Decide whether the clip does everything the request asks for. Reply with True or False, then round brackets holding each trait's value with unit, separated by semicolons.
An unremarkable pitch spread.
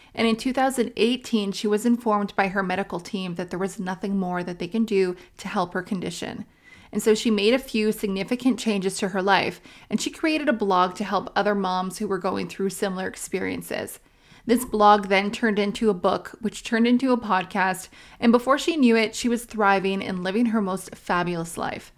True (3.1 semitones)